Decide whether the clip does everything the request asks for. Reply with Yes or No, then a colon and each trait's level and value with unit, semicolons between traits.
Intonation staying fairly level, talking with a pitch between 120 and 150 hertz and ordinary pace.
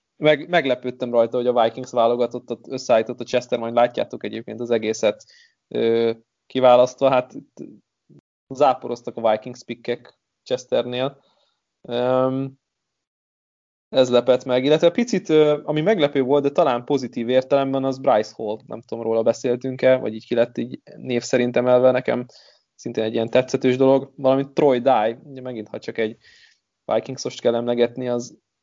Yes: narrow, 2.1 semitones; low, 125 Hz; average, 140 wpm